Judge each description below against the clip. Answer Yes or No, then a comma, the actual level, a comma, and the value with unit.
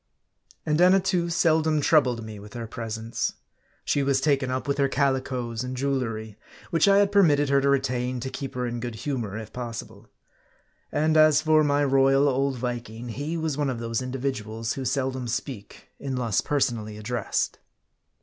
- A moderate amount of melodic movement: Yes, average, 3.7 semitones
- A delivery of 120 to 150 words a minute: No, average, 170 wpm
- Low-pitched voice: Yes, low, 130 Hz